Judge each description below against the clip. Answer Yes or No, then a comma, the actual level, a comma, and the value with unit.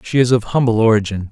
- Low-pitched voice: Yes, low, 115 Hz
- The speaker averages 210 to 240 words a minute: Yes, fast, 230 wpm